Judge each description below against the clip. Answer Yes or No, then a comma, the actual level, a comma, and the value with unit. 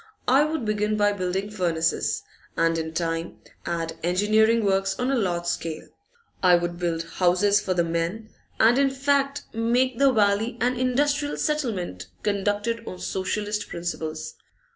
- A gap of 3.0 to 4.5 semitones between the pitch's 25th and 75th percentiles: No, average, 5.2 semitones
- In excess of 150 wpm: No, average, 145 wpm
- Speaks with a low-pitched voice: No, high, 205 Hz